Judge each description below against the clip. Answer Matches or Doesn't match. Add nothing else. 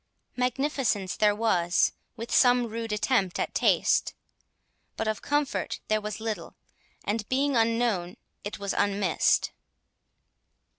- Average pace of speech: Doesn't match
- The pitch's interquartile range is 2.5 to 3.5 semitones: Matches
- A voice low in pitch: Doesn't match